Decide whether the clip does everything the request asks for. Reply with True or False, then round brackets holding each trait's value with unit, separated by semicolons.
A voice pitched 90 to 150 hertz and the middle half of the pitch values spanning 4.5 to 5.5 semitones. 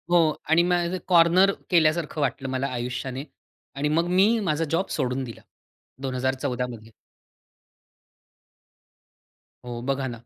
True (140 Hz; 4.9 semitones)